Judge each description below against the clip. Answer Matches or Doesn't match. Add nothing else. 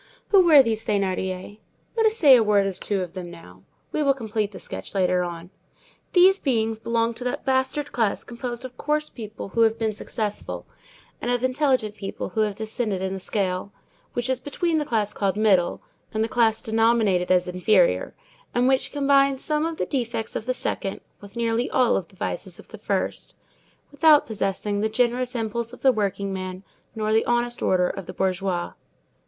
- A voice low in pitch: Doesn't match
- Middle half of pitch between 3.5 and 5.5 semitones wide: Matches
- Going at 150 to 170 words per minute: Doesn't match